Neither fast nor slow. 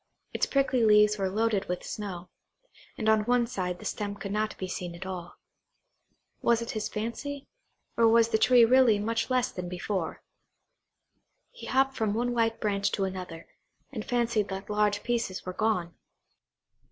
Yes: average, 165 wpm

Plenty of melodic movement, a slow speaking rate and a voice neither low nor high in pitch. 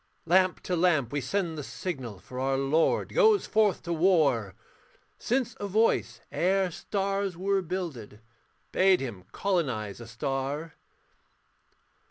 Yes: wide, 6.4 semitones; slow, 130 wpm; medium, 165 Hz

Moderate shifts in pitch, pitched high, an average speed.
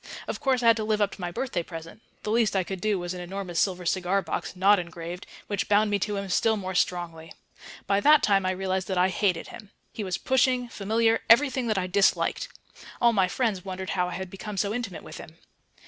No: average, 3.0 semitones; high, 195 Hz; fast, 230 wpm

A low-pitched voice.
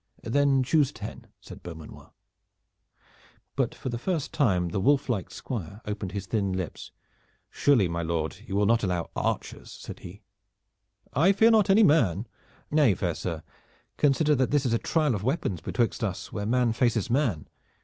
Yes: low, 115 Hz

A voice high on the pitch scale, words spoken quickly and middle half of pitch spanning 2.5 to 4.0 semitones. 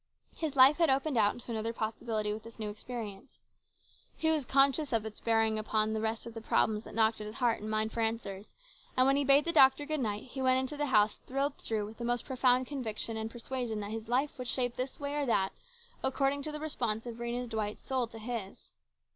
Yes: high, 235 Hz; fast, 235 wpm; average, 3.5 semitones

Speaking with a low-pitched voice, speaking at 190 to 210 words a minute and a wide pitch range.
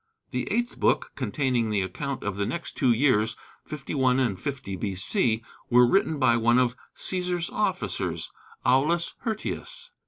No: low, 130 Hz; average, 145 wpm; wide, 6.5 semitones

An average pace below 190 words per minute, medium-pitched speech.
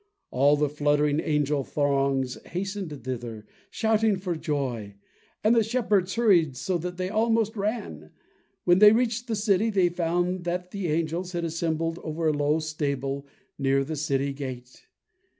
Yes: average, 150 wpm; medium, 165 Hz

